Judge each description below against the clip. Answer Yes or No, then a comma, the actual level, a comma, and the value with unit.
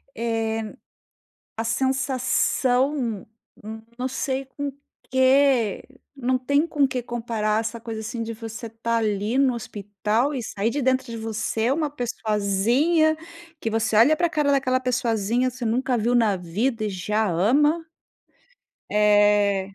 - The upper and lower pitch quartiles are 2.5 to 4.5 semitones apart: Yes, average, 3.3 semitones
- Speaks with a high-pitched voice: Yes, high, 235 Hz